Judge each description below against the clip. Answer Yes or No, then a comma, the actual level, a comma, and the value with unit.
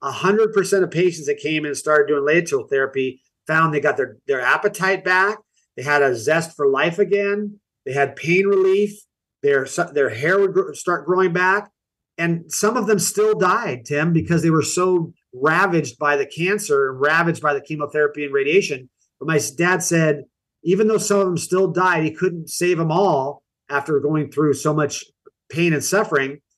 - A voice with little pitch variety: No, average, 5.1 semitones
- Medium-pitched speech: Yes, medium, 170 Hz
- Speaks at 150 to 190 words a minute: Yes, average, 185 wpm